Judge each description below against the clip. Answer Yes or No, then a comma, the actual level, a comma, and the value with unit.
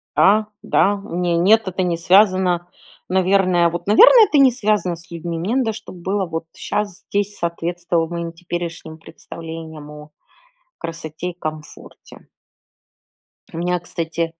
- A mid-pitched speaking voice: Yes, medium, 175 Hz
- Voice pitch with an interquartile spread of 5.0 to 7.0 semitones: No, average, 2.9 semitones